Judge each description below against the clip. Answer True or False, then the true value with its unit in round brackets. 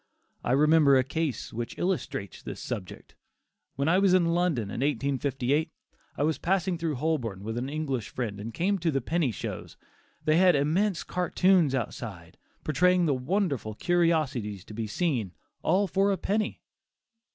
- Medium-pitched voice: True (150 Hz)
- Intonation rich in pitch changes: True (6.0 semitones)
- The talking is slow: False (160 wpm)